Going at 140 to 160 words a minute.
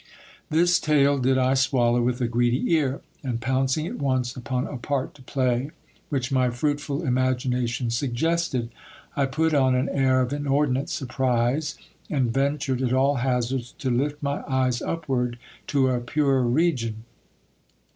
Yes: average, 150 wpm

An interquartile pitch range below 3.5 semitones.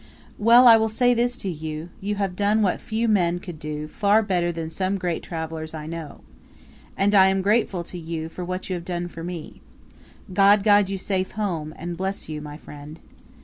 No: average, 3.8 semitones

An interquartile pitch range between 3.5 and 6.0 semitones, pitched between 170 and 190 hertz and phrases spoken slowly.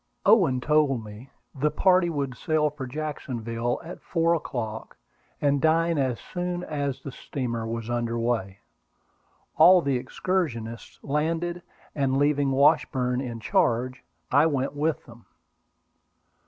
No: average, 4.6 semitones; medium, 140 Hz; slow, 130 wpm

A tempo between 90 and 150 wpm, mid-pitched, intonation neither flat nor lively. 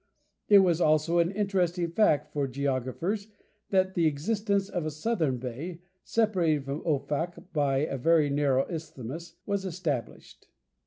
Yes: average, 140 wpm; medium, 165 Hz; average, 4.7 semitones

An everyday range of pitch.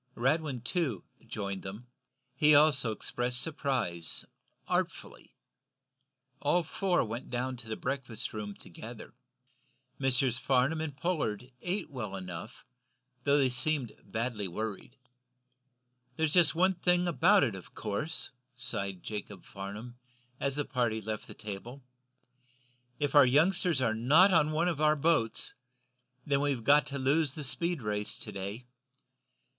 No: wide, 5.7 semitones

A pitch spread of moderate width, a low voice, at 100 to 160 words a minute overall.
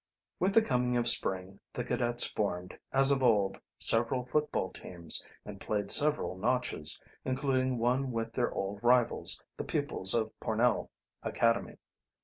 Yes: average, 4.0 semitones; low, 120 Hz; average, 140 wpm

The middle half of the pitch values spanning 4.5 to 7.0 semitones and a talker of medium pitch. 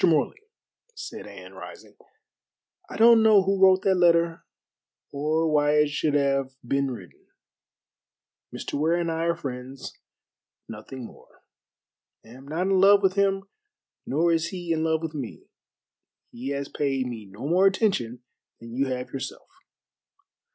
Yes: average, 5.3 semitones; medium, 155 Hz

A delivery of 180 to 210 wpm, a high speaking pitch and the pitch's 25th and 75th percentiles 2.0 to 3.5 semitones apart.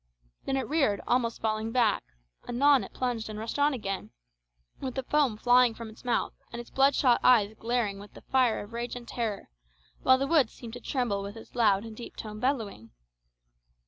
Yes: average, 195 wpm; high, 235 Hz; average, 2.9 semitones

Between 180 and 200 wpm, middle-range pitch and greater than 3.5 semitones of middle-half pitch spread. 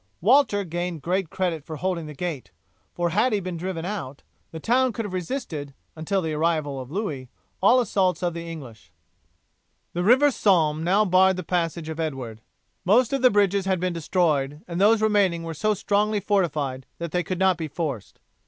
Yes: average, 190 wpm; medium, 175 Hz; average, 4.2 semitones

